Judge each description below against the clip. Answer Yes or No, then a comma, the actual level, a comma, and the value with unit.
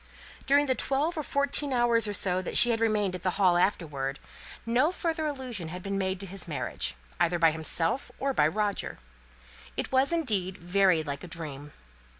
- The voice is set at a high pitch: Yes, high, 195 Hz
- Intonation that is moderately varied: No, wide, 7.1 semitones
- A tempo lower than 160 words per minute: No, average, 175 wpm